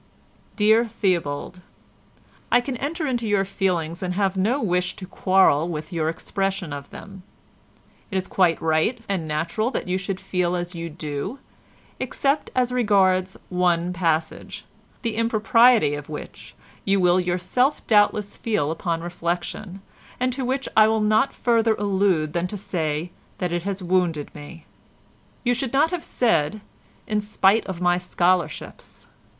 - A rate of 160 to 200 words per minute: No, average, 150 wpm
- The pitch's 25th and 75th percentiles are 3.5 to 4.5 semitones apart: Yes, average, 4.1 semitones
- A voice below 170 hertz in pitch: No, medium, 185 Hz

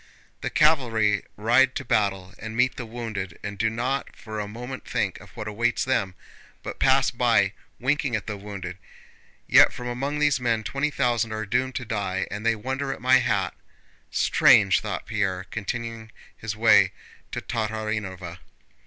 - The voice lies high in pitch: No, low, 115 Hz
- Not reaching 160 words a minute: No, average, 165 wpm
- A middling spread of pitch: Yes, average, 3.2 semitones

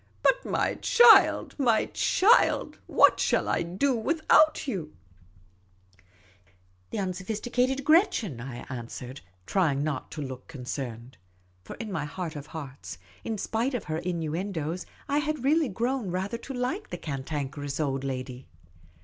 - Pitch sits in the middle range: Yes, medium, 165 Hz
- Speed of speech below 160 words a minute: Yes, average, 150 wpm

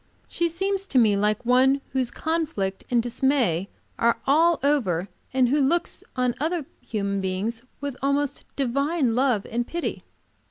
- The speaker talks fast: No, average, 155 wpm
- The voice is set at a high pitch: Yes, very high, 260 Hz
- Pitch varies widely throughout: No, average, 4.5 semitones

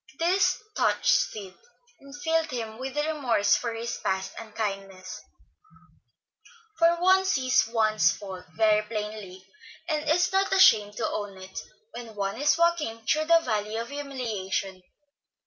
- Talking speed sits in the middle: No, slow, 130 wpm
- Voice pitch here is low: No, high, 230 Hz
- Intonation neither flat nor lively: No, wide, 6.9 semitones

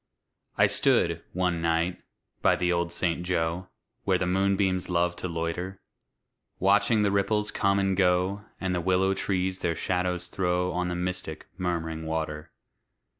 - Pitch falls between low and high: No, very low, 90 Hz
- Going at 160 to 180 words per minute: No, average, 150 wpm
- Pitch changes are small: Yes, narrow, 1.7 semitones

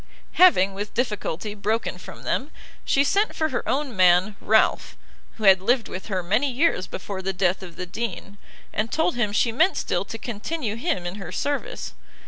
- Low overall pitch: No, high, 215 Hz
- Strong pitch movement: Yes, wide, 5.7 semitones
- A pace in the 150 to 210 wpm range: Yes, average, 185 wpm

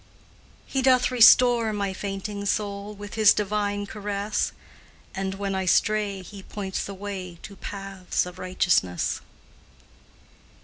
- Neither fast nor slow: No, slow, 125 wpm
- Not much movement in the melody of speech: Yes, narrow, 1.6 semitones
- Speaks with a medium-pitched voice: No, high, 200 Hz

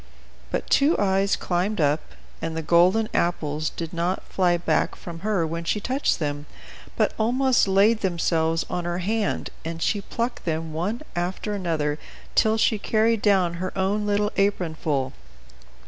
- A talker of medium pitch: Yes, medium, 180 Hz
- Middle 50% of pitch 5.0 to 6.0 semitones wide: No, average, 4.0 semitones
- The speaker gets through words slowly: No, average, 160 wpm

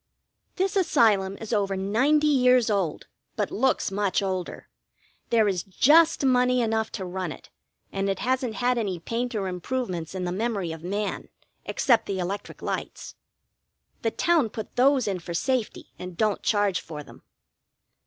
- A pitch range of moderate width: Yes, average, 4.8 semitones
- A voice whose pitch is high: Yes, high, 210 Hz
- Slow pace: No, average, 165 wpm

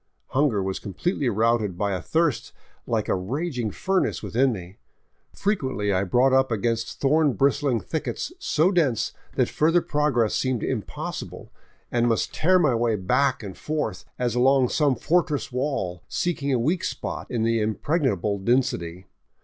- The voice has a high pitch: No, low, 125 Hz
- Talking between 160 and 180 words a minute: No, average, 150 wpm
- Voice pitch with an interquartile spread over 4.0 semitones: Yes, wide, 5.6 semitones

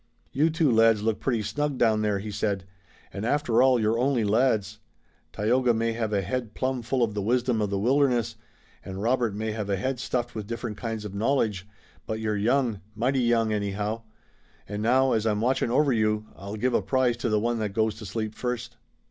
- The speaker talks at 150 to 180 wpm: No, fast, 205 wpm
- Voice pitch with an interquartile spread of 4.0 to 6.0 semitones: No, average, 2.8 semitones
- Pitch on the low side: Yes, low, 115 Hz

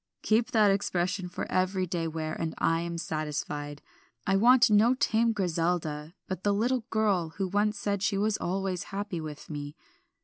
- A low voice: No, medium, 185 Hz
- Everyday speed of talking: Yes, average, 170 wpm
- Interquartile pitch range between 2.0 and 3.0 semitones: No, average, 4.1 semitones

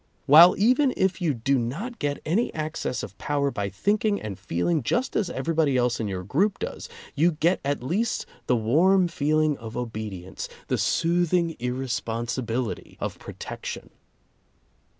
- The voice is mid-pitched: Yes, medium, 145 Hz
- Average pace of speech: Yes, average, 150 wpm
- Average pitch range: No, wide, 6.9 semitones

